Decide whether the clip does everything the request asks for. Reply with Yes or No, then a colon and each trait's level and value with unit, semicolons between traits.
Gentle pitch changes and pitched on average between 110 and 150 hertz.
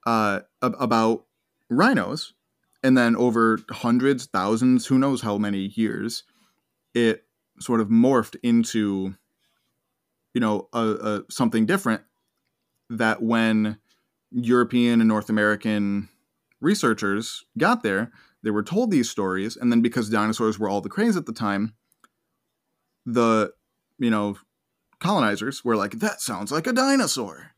Yes: narrow, 2.3 semitones; low, 115 Hz